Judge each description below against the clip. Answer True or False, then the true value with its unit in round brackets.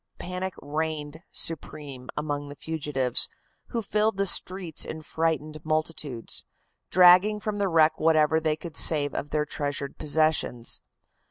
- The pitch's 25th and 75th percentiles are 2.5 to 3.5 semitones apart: True (2.8 semitones)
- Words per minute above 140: False (135 wpm)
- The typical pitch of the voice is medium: True (155 Hz)